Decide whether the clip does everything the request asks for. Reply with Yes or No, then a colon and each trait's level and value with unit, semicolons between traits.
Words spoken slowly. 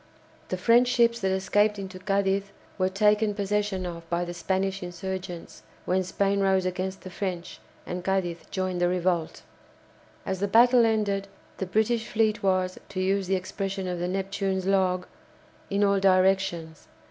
No: average, 160 wpm